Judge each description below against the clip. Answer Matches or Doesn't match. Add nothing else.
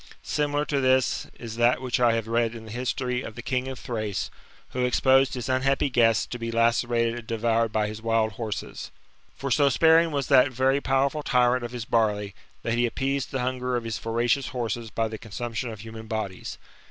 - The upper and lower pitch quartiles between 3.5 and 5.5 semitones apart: Doesn't match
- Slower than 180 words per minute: Doesn't match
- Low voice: Matches